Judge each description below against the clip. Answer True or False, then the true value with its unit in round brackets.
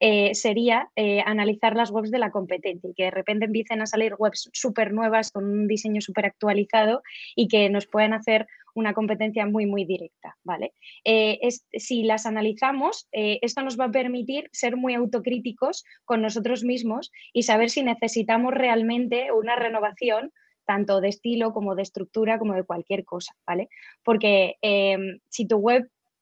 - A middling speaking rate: True (170 wpm)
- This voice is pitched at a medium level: False (220 Hz)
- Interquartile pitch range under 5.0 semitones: True (2.5 semitones)